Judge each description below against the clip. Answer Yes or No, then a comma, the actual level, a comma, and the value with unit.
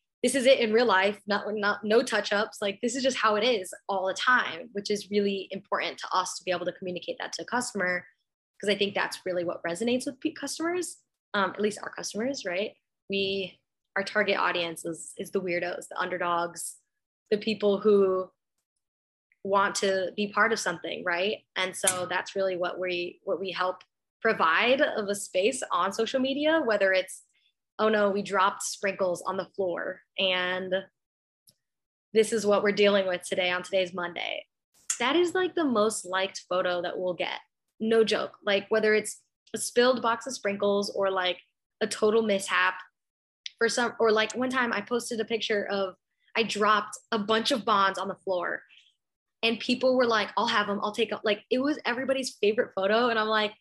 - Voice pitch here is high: Yes, high, 205 Hz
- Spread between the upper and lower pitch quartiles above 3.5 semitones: No, average, 3.2 semitones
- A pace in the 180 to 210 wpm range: Yes, average, 195 wpm